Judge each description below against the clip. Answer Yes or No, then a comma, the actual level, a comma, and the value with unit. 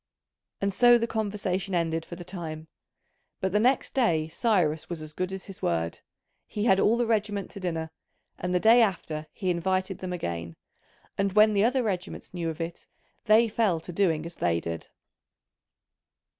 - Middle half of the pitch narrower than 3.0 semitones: No, average, 4.2 semitones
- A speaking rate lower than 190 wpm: Yes, average, 180 wpm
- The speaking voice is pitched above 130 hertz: Yes, medium, 185 Hz